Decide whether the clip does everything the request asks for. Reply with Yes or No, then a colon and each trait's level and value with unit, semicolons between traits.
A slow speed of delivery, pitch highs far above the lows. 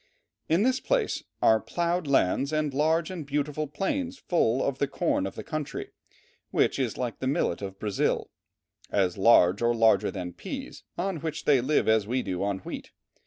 No: average, 180 wpm; wide, 6.7 semitones